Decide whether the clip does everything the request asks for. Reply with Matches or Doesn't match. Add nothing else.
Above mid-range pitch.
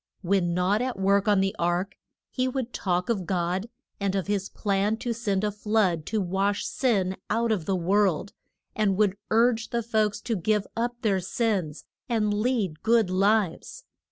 Matches